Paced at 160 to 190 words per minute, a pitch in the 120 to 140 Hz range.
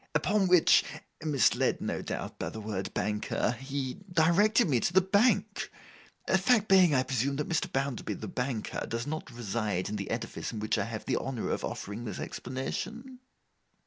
Yes: average, 175 wpm; low, 135 Hz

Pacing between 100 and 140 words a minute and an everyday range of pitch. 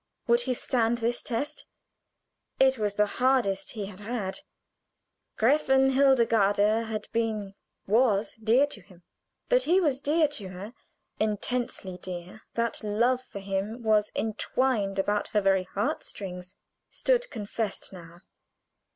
Yes: slow, 135 wpm; average, 4.2 semitones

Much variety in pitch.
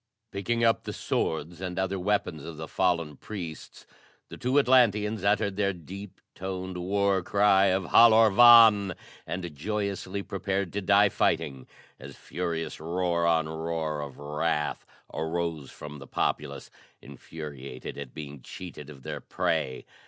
No: average, 4.3 semitones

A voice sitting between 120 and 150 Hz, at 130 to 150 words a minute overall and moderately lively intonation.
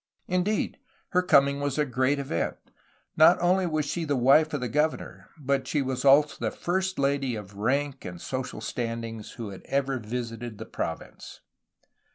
No: medium, 140 Hz; average, 170 wpm; average, 3.9 semitones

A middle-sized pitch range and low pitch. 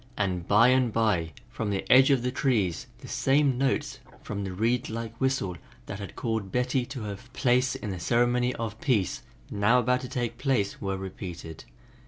Yes: average, 4.1 semitones; low, 115 Hz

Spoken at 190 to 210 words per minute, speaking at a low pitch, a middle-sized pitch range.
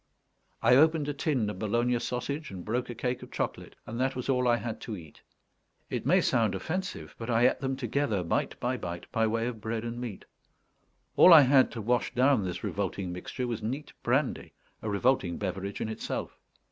Yes: average, 200 wpm; low, 120 Hz; average, 3.7 semitones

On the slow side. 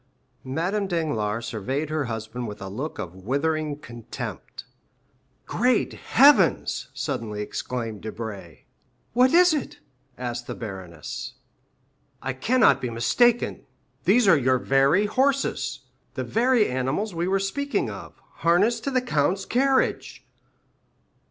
Yes: slow, 120 wpm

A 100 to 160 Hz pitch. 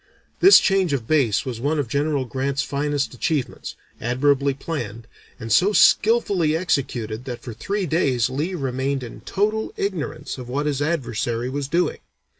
Yes: medium, 140 Hz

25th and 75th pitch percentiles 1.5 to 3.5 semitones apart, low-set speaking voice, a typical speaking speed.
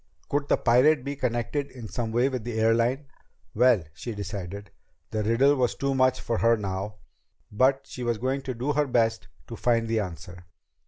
Yes: average, 3.1 semitones; low, 120 Hz; average, 190 wpm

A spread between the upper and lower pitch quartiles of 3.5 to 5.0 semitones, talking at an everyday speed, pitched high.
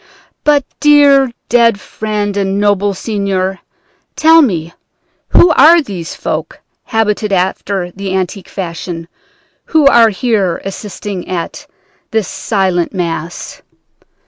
No: average, 3.9 semitones; slow, 110 wpm; high, 200 Hz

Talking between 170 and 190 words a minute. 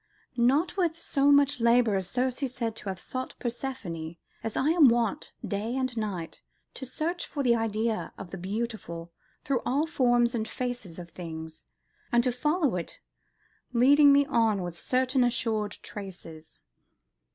No: average, 155 wpm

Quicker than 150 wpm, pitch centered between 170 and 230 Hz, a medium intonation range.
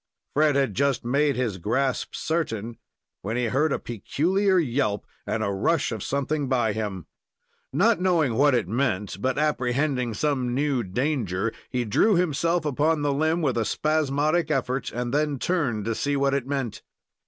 No: average, 165 wpm; low, 135 Hz; average, 4.4 semitones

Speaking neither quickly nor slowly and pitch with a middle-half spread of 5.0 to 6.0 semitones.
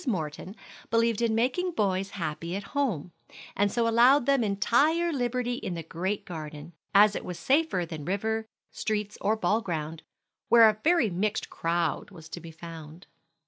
Yes: average, 165 wpm; wide, 5.6 semitones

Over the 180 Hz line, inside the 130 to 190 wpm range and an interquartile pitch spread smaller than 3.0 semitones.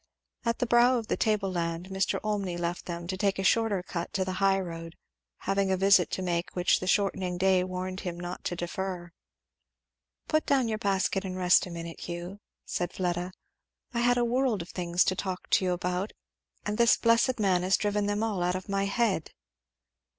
No: high, 190 Hz; average, 200 wpm; narrow, 2.6 semitones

